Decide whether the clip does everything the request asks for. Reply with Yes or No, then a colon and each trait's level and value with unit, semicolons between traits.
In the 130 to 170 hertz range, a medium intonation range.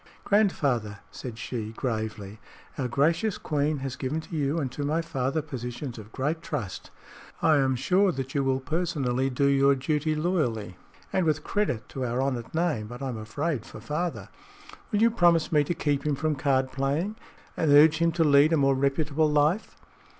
Yes: medium, 140 Hz; average, 3.7 semitones